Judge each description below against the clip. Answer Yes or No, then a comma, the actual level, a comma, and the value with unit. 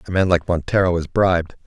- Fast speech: Yes, fast, 215 wpm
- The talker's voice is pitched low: Yes, very low, 90 Hz